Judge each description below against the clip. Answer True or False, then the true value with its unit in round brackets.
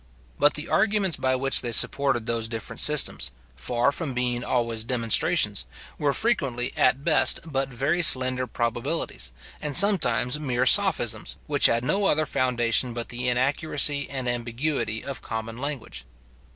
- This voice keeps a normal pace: True (145 wpm)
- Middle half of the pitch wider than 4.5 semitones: False (3.8 semitones)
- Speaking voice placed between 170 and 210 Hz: False (130 Hz)